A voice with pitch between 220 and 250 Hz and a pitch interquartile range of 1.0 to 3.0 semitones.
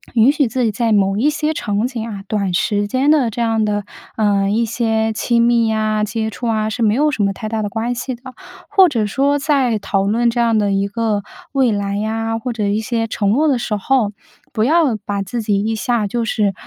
Yes: high, 225 Hz; narrow, 2.6 semitones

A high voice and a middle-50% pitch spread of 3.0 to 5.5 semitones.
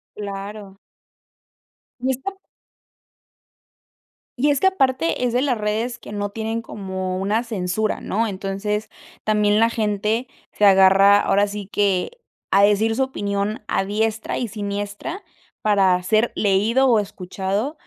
No: high, 210 Hz; narrow, 2.5 semitones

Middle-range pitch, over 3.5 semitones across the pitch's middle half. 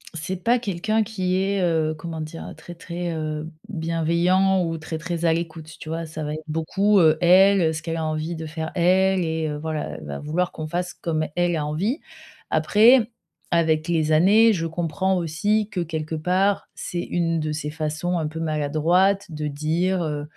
No: medium, 165 Hz; average, 2.8 semitones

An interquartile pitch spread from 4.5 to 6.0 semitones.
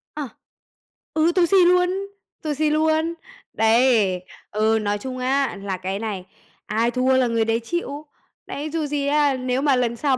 Yes: average, 5.2 semitones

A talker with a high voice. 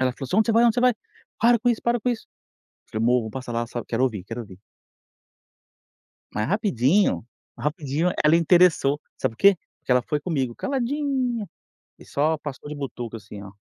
No: medium, 150 Hz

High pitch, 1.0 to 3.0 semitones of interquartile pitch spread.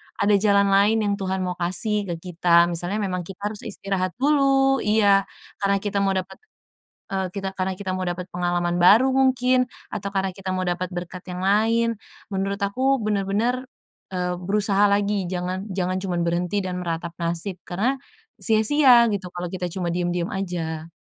Yes: high, 195 Hz; average, 2.7 semitones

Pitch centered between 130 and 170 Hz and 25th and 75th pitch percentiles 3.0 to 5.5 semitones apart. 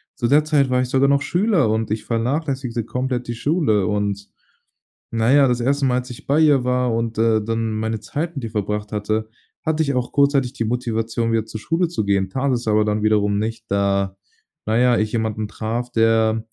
No: low, 115 Hz; average, 3.5 semitones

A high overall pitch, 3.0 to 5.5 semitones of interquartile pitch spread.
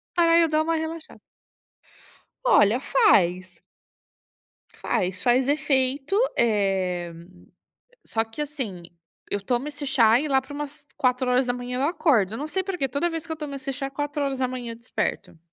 Yes: very high, 265 Hz; average, 4.6 semitones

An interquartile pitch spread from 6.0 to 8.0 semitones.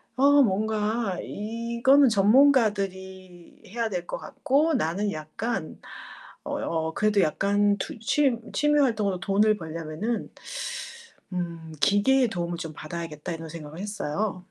No: average, 5.1 semitones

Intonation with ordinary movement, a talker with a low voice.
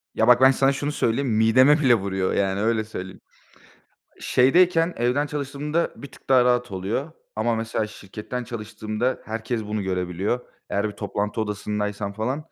Yes: average, 4.2 semitones; low, 115 Hz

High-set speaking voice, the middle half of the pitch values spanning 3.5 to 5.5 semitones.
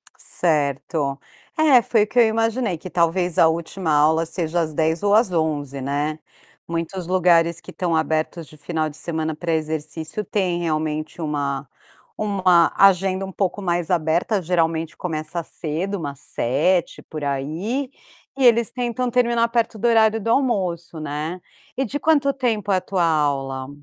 No: medium, 170 Hz; average, 4.7 semitones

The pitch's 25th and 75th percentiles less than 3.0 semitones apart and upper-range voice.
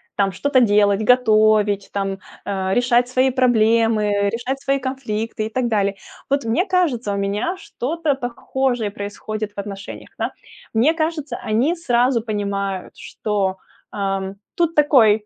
No: average, 4.4 semitones; high, 225 Hz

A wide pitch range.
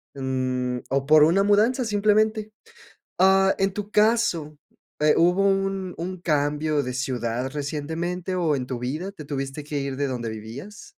Yes: wide, 6.1 semitones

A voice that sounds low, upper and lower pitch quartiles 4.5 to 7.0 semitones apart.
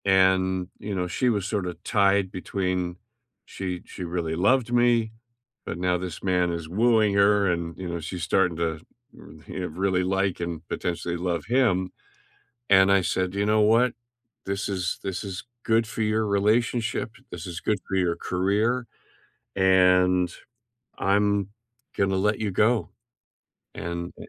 No: very low, 95 Hz; narrow, 2.6 semitones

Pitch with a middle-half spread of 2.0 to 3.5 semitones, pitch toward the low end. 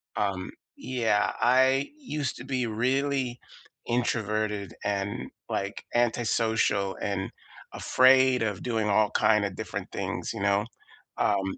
No: average, 3.9 semitones; low, 110 Hz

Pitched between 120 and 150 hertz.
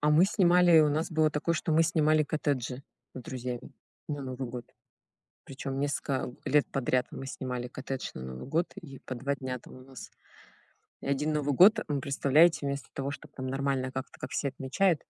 Yes: medium, 140 Hz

